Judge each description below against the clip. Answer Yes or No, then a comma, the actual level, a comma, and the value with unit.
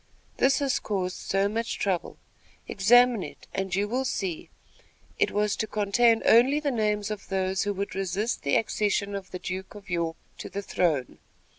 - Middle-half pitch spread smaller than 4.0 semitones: Yes, average, 2.9 semitones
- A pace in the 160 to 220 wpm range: Yes, average, 175 wpm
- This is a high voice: Yes, high, 200 Hz